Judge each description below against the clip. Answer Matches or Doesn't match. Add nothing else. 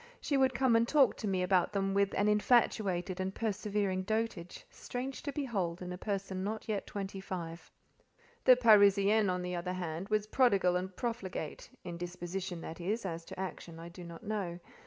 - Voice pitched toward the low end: Doesn't match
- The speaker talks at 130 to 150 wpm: Doesn't match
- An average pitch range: Matches